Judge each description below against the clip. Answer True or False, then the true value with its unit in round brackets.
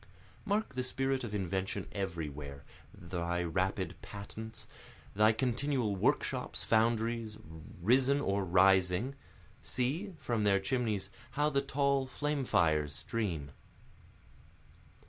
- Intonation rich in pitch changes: True (5.9 semitones)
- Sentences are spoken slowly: True (105 wpm)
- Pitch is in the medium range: False (110 Hz)